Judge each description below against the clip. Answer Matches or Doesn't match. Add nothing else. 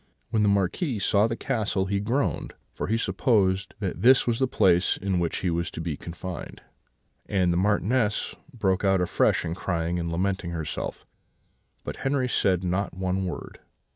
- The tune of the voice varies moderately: Matches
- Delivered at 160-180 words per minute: Matches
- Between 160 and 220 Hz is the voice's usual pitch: Doesn't match